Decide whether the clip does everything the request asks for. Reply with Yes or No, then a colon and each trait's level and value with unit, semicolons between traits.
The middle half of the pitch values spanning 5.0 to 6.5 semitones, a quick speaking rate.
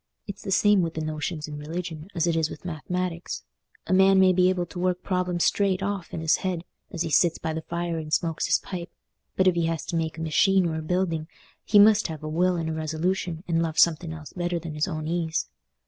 No: narrow, 2.4 semitones; fast, 235 wpm